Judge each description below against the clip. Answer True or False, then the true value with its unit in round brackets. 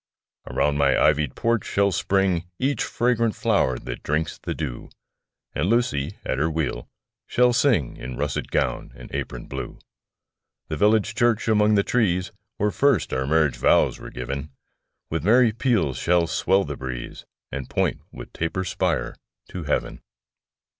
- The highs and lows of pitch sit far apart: True (7.5 semitones)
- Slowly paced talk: False (155 wpm)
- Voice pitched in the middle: False (85 Hz)